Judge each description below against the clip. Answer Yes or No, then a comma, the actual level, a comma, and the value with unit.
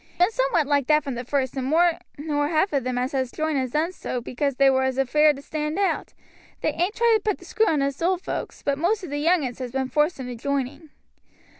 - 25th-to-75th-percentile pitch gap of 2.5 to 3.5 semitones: No, average, 4.0 semitones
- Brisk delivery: Yes, fast, 255 wpm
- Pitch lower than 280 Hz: No, very high, 290 Hz